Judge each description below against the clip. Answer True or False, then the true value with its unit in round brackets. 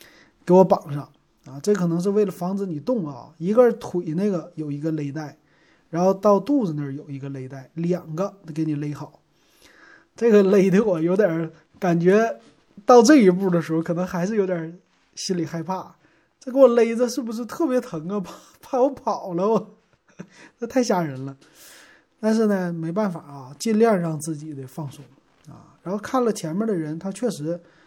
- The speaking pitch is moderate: True (180 Hz)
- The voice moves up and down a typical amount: True (5.0 semitones)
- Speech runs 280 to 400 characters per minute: False (265 characters per minute)